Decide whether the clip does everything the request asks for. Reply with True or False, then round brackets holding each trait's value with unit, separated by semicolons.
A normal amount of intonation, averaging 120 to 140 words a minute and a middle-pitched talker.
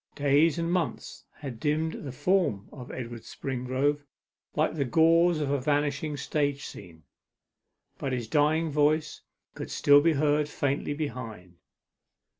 True (3.0 semitones; 135 wpm; 145 Hz)